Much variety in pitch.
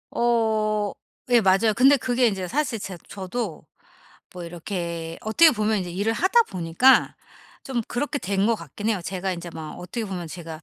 No: average, 5.0 semitones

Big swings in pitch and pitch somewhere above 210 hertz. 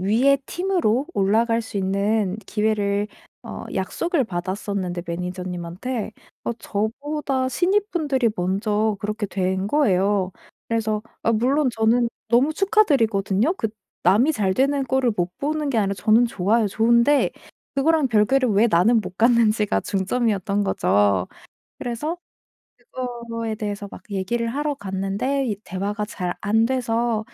No: average, 4.5 semitones; high, 220 Hz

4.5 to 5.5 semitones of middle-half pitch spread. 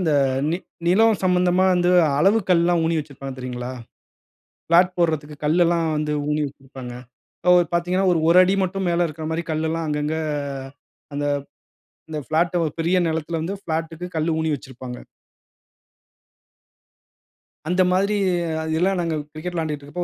No: average, 2.7 semitones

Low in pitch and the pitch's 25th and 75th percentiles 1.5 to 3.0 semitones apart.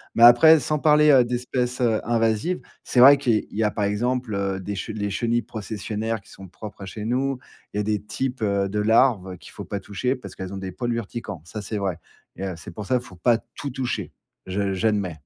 No: low, 110 Hz; average, 3.7 semitones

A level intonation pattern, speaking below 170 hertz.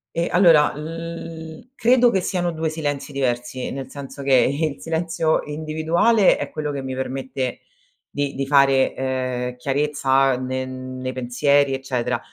No: average, 3.5 semitones; medium, 140 Hz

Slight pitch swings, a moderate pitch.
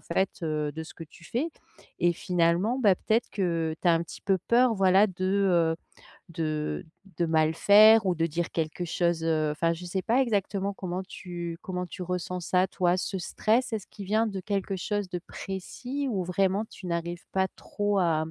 No: average, 3.1 semitones; medium, 180 Hz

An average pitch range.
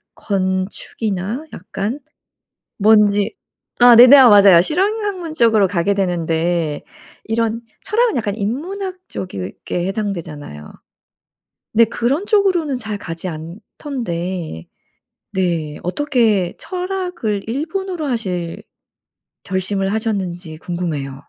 No: wide, 7.1 semitones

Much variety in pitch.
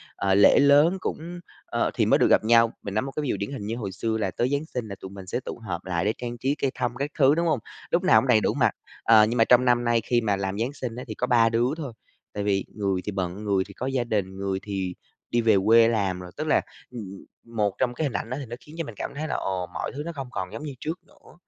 No: average, 5.0 semitones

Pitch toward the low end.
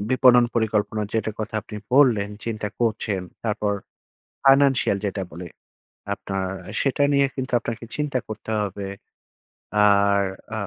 Yes: low, 110 Hz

